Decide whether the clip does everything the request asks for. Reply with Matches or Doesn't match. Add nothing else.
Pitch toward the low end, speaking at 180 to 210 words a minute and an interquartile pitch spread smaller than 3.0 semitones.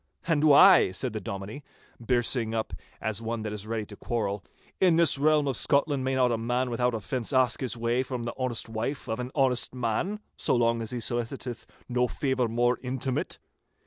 Matches